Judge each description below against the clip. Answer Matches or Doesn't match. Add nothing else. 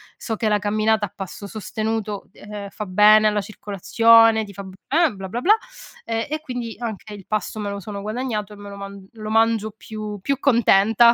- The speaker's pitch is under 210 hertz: Doesn't match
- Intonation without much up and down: Matches